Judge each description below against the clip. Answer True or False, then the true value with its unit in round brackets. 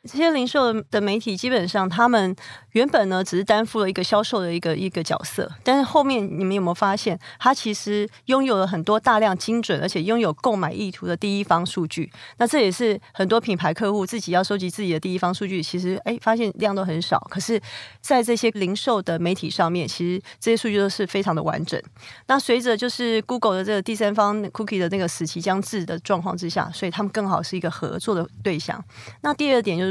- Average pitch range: True (3.8 semitones)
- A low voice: False (200 Hz)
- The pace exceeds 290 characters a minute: True (360 characters per minute)